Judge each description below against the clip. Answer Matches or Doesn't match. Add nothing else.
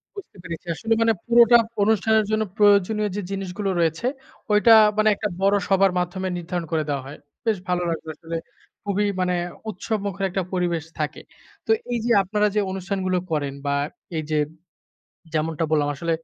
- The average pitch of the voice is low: Doesn't match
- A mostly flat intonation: Doesn't match